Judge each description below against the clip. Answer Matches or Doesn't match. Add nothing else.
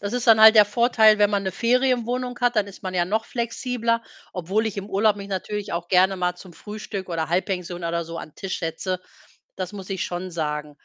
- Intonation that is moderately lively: Matches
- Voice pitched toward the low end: Doesn't match